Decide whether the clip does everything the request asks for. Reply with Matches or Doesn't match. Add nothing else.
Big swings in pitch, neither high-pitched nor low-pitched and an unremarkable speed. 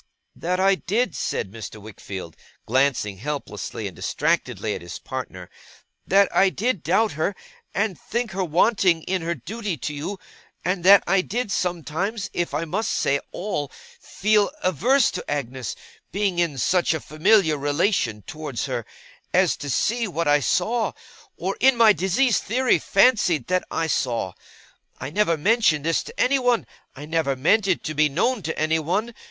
Matches